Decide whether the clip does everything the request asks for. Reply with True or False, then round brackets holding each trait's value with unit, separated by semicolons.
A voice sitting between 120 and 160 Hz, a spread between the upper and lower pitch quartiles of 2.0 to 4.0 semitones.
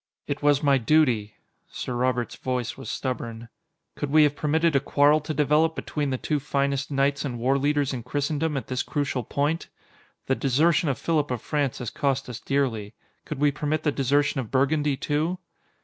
True (140 Hz; 2.4 semitones)